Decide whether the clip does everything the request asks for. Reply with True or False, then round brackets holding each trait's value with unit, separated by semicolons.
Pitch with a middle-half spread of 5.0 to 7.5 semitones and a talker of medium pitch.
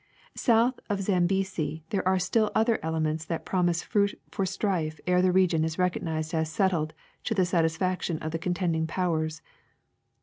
False (2.9 semitones; 180 Hz)